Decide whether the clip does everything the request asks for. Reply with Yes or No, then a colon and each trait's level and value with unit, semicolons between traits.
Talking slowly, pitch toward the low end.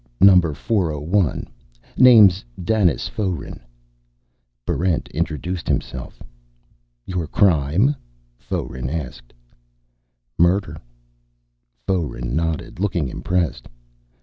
Yes: slow, 70 wpm; very low, 85 Hz